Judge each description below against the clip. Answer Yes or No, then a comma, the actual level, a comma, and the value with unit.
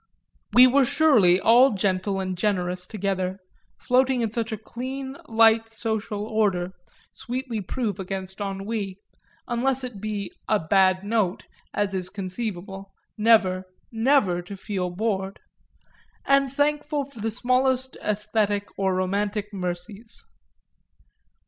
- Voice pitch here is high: Yes, high, 210 Hz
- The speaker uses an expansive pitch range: No, average, 3.9 semitones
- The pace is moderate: No, slow, 120 wpm